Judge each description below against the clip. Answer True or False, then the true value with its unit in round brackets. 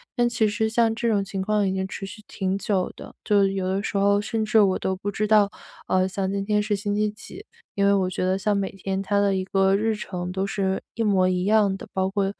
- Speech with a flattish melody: True (1.8 semitones)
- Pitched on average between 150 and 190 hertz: False (200 Hz)